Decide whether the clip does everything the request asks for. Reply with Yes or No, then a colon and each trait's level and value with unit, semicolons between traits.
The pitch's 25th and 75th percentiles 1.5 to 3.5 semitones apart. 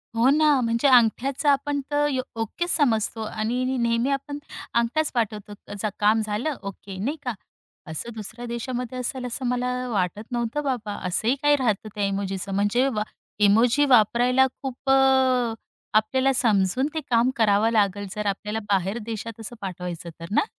No: average, 3.9 semitones